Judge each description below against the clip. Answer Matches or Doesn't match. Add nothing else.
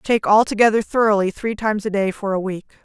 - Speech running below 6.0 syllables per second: Doesn't match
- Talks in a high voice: Matches